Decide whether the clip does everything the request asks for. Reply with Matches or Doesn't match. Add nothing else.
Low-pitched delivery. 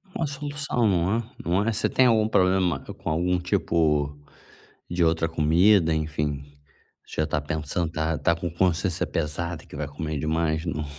Matches